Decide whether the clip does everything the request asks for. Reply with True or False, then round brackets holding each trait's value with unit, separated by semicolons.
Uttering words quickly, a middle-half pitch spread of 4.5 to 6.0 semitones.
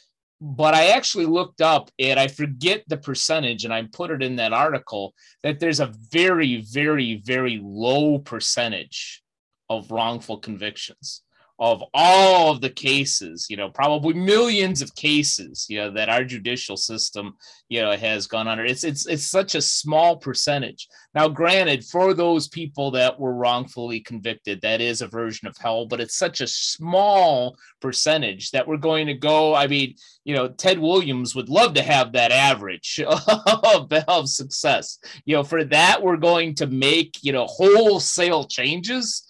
False (170 wpm; 5.4 semitones)